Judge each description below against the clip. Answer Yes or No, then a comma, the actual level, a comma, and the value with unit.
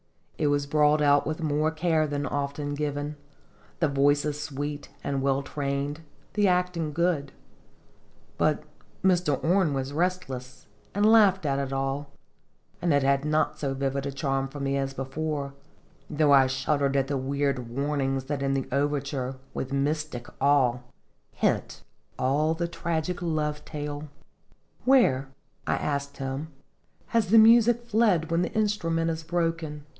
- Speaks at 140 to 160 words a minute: Yes, average, 150 wpm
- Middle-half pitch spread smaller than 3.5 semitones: Yes, average, 3.0 semitones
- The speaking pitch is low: No, medium, 145 Hz